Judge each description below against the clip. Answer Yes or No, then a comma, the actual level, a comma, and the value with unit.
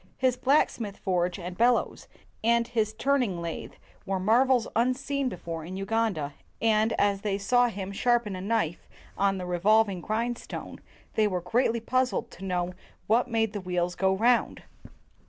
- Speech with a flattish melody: No, average, 4.2 semitones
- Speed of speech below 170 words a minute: Yes, average, 155 wpm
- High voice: Yes, high, 215 Hz